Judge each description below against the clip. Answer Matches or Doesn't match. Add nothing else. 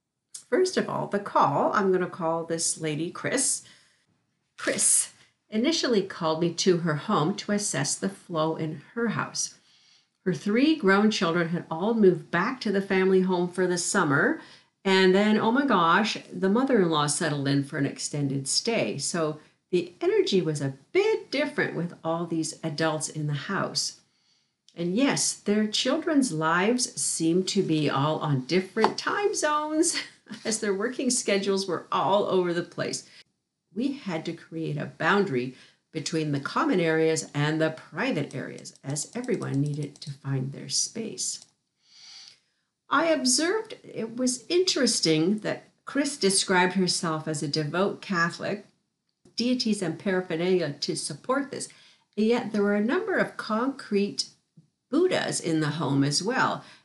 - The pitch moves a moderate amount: Doesn't match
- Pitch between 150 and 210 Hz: Matches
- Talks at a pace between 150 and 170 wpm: Matches